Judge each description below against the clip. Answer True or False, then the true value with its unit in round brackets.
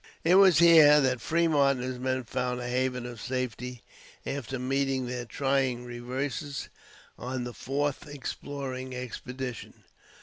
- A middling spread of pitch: False (2.0 semitones)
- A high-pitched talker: False (130 Hz)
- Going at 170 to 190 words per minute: False (135 wpm)